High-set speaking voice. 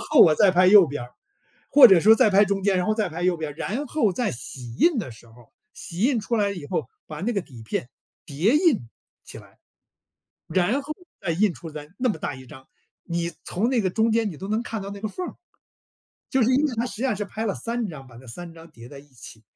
Yes: high, 195 Hz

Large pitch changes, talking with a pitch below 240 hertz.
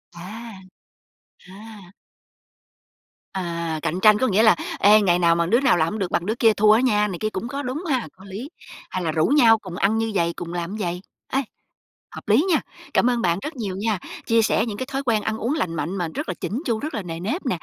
No: average, 4.6 semitones; high, 210 Hz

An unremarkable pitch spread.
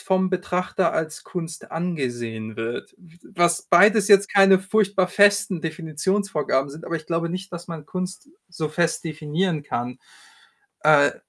Yes: average, 3.5 semitones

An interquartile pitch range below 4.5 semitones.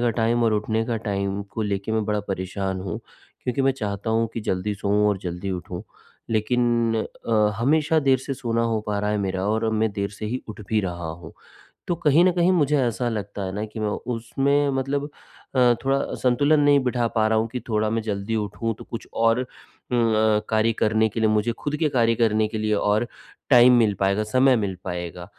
Yes: average, 3.1 semitones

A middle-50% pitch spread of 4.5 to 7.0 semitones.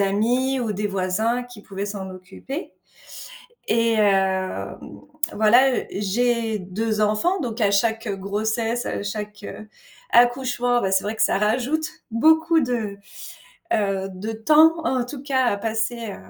No: average, 3.5 semitones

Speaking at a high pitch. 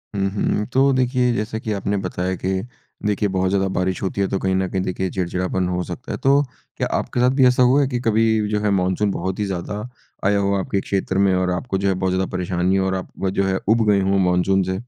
No: very low, 95 Hz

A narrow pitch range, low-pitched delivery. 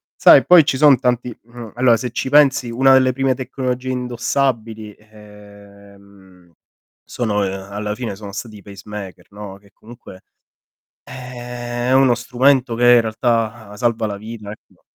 No: average, 3.4 semitones; low, 115 Hz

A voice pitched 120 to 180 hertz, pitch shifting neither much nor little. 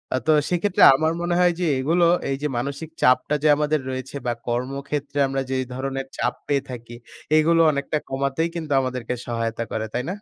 Yes: medium, 140 Hz; average, 3.4 semitones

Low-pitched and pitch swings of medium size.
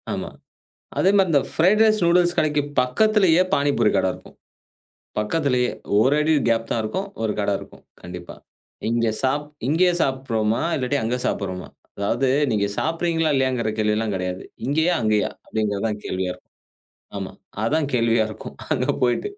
No: low, 125 Hz; wide, 6.7 semitones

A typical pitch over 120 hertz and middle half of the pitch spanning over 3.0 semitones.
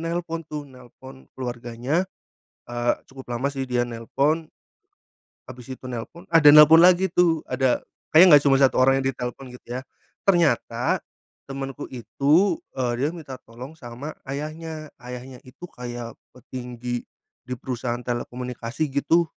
Yes: low, 135 Hz; average, 4.0 semitones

